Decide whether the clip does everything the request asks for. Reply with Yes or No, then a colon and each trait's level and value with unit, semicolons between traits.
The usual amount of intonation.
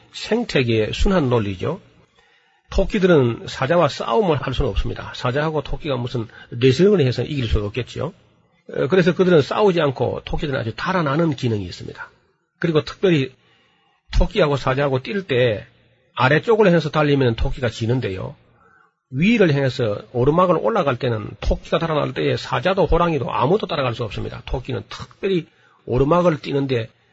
No: wide, 6.0 semitones